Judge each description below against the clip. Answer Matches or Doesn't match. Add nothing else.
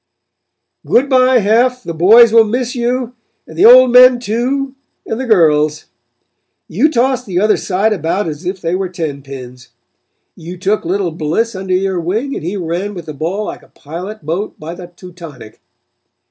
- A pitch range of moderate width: Doesn't match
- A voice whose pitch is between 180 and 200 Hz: Matches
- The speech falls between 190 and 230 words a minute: Doesn't match